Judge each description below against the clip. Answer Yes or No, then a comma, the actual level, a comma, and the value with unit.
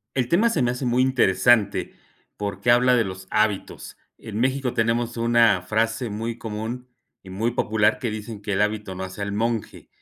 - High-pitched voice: No, low, 115 Hz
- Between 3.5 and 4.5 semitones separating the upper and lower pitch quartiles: No, average, 2.8 semitones